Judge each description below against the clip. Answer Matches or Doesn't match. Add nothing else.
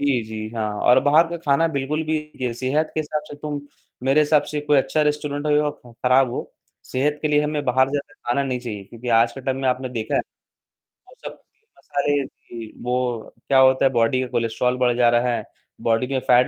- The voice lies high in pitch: Doesn't match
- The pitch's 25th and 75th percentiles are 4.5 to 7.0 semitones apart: Doesn't match